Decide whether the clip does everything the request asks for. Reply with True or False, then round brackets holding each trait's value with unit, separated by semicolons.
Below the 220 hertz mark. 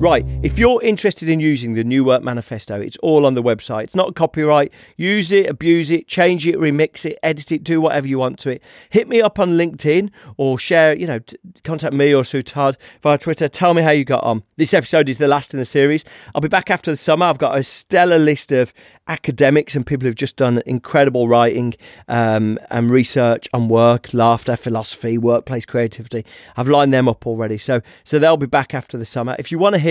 True (140 Hz)